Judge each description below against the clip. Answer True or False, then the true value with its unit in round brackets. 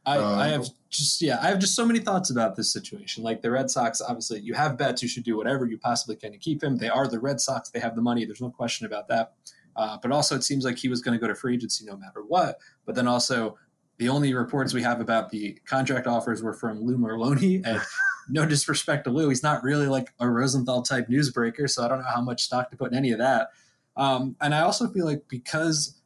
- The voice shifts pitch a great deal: False (3.6 semitones)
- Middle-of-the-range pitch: False (130 Hz)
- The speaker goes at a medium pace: False (260 wpm)